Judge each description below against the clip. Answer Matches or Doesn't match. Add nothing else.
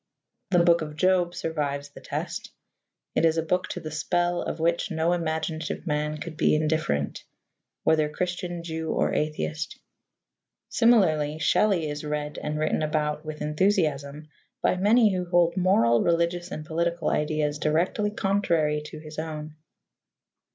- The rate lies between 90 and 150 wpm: Matches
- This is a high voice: Doesn't match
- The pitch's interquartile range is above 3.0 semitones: Doesn't match